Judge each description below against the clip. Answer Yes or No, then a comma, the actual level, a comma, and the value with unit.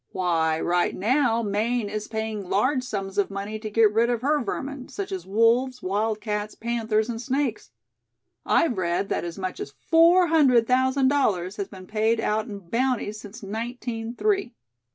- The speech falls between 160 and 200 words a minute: Yes, average, 170 wpm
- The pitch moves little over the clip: No, average, 3.8 semitones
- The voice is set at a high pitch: Yes, high, 225 Hz